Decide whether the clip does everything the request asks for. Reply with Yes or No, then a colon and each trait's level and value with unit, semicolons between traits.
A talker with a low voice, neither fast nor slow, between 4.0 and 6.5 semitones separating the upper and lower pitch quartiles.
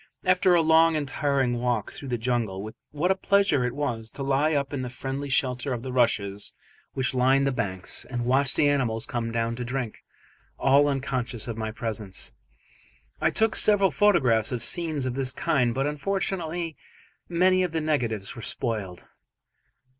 Yes: low, 130 Hz; average, 175 wpm; average, 4.4 semitones